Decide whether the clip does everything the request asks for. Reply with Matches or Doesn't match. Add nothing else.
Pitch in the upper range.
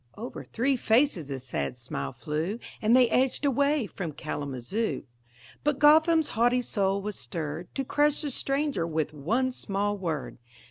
Matches